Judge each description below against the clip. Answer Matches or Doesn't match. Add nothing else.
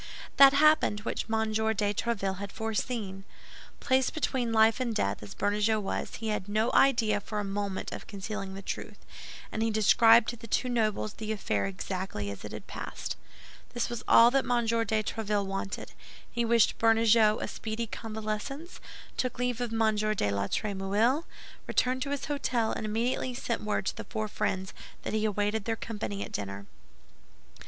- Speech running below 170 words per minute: Doesn't match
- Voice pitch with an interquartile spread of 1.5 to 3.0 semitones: Matches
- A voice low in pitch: Doesn't match